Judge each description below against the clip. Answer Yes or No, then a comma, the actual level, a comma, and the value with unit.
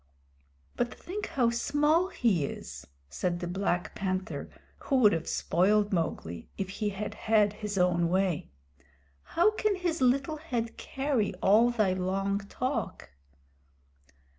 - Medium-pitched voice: No, high, 210 Hz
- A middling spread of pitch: No, wide, 5.8 semitones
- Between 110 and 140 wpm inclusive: Yes, slow, 135 wpm